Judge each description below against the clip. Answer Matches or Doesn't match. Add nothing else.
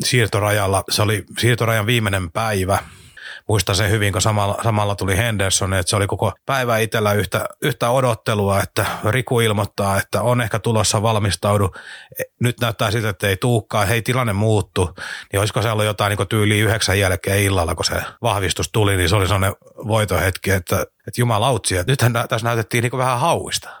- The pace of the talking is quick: Matches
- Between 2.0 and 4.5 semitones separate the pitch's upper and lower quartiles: Matches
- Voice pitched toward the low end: Matches